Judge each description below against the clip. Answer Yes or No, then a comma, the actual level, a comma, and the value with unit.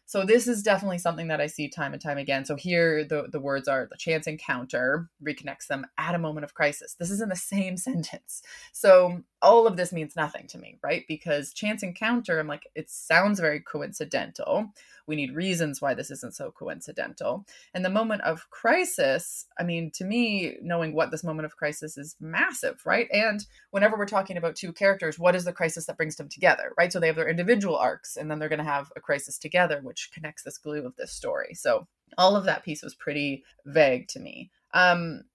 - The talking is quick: Yes, fast, 215 wpm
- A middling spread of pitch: Yes, average, 4.3 semitones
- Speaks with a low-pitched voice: No, medium, 170 Hz